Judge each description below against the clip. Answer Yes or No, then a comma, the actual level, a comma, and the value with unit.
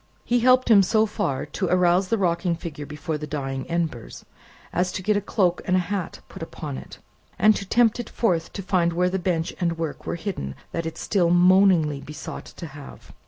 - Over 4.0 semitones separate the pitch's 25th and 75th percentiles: No, average, 3.5 semitones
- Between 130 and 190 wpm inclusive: No, fast, 205 wpm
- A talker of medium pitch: Yes, medium, 175 Hz